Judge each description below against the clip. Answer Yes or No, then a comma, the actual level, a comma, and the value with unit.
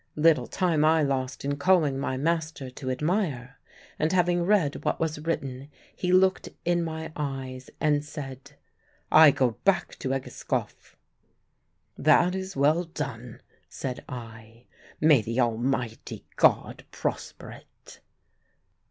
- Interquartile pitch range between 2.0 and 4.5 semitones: Yes, average, 4.2 semitones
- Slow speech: Yes, slow, 125 wpm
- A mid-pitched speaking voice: Yes, medium, 145 Hz